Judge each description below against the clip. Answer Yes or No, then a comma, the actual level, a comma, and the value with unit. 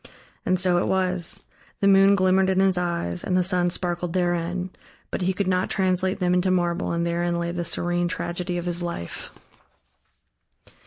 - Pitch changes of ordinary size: No, narrow, 1.3 semitones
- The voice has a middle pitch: Yes, medium, 180 Hz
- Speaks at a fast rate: No, average, 175 wpm